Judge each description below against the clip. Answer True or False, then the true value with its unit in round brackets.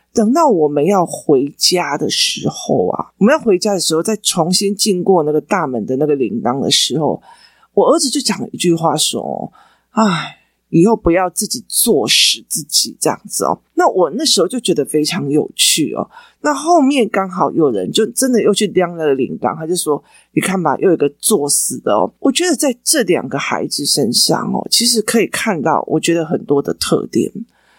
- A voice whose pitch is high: True (195 Hz)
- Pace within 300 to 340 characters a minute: False (280 characters per minute)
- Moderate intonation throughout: False (6.4 semitones)